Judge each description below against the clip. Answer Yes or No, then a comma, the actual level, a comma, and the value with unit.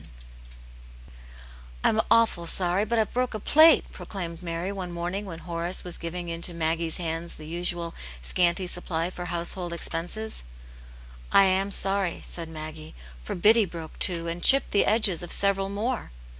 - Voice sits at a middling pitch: Yes, medium, 175 Hz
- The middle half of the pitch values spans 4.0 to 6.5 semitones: No, average, 2.9 semitones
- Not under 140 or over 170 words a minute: Yes, average, 165 wpm